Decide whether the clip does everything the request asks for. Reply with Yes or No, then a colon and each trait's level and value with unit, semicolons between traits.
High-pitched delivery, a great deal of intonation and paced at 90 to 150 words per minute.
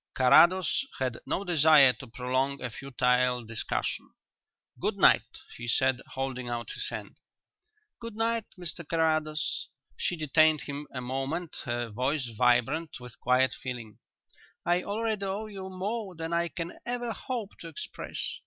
No: medium, 150 Hz; wide, 6.1 semitones; average, 145 wpm